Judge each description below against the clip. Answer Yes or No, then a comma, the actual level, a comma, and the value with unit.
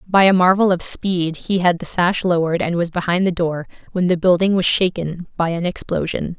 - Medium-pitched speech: Yes, medium, 175 Hz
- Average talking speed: No, fast, 215 wpm